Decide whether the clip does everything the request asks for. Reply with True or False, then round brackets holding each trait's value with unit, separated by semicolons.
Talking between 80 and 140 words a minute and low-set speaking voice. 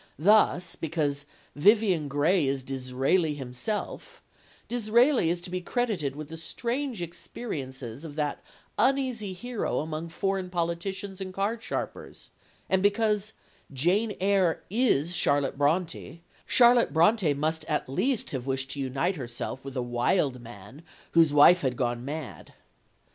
False (135 wpm; 165 Hz)